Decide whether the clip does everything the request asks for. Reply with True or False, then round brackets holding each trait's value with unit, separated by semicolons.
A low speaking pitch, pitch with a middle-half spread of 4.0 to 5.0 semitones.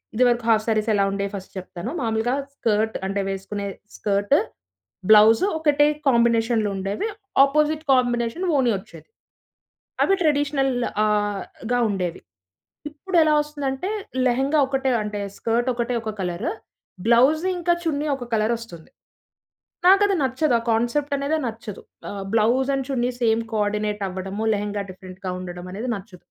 False (230 Hz; 4.7 semitones)